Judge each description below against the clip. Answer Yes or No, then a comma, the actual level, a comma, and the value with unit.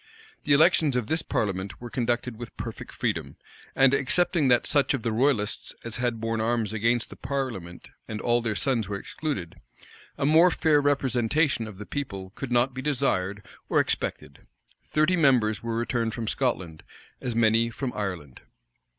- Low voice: Yes, low, 120 Hz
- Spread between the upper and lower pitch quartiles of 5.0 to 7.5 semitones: No, average, 4.1 semitones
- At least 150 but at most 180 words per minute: Yes, average, 165 wpm